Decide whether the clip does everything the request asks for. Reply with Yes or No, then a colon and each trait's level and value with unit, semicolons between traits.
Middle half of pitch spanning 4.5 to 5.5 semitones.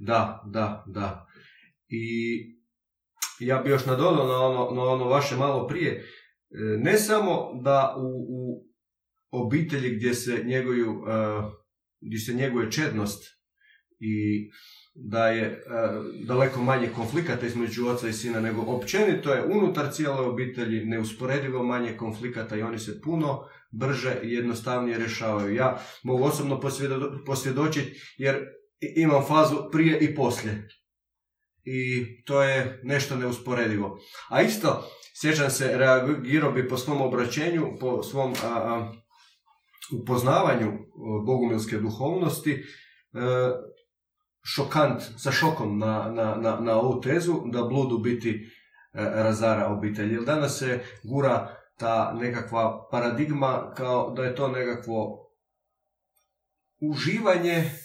No: average, 3.5 semitones